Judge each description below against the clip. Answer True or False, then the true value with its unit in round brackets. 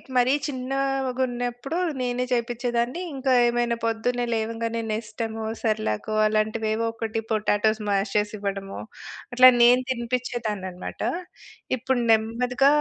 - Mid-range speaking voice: False (235 Hz)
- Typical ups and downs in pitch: False (2.3 semitones)